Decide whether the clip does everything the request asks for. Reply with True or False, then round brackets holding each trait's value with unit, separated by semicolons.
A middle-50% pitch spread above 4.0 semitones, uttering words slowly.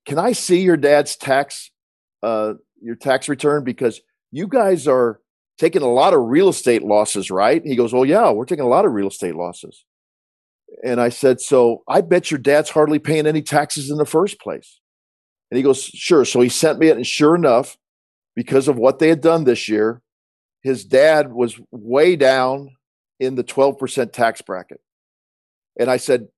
False (4.4 semitones; 190 wpm)